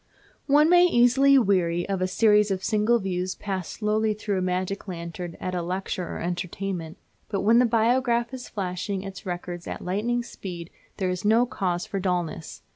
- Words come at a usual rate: Yes, average, 180 wpm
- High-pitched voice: Yes, high, 195 Hz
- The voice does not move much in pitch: No, average, 3.9 semitones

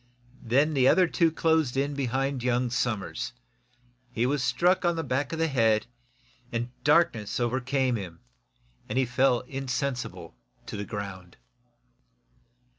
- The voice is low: Yes, low, 130 Hz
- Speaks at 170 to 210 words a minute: No, average, 140 wpm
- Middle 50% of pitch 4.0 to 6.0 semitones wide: No, average, 3.3 semitones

